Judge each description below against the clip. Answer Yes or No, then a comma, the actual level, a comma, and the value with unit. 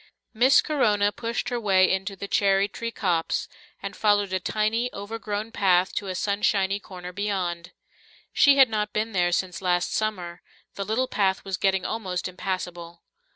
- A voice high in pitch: Yes, high, 200 Hz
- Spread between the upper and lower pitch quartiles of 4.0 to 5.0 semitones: No, average, 2.7 semitones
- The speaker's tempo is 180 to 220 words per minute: No, average, 160 wpm